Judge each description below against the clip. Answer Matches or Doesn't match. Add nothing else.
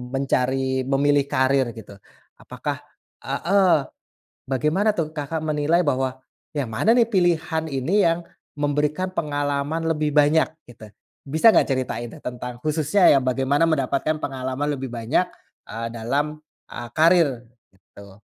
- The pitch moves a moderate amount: Matches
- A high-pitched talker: Doesn't match